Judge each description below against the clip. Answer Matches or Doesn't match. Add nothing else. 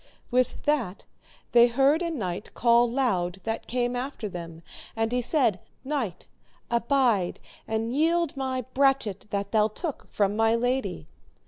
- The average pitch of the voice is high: Matches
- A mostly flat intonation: Doesn't match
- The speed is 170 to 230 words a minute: Doesn't match